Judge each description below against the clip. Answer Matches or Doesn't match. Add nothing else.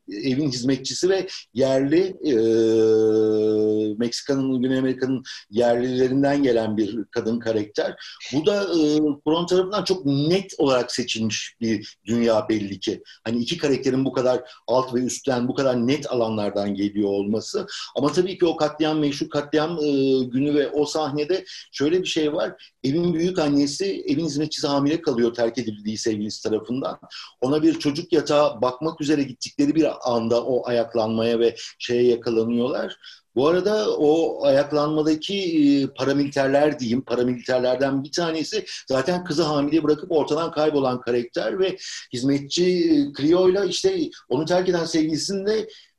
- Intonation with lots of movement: Doesn't match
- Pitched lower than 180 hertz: Matches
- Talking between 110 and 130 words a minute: Doesn't match